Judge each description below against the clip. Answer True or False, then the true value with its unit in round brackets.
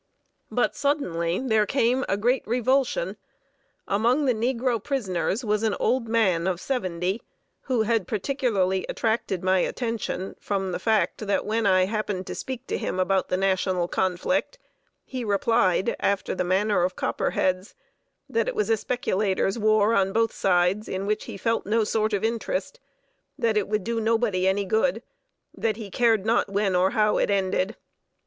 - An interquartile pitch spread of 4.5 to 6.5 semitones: False (3.4 semitones)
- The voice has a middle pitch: False (210 Hz)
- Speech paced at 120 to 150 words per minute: False (165 wpm)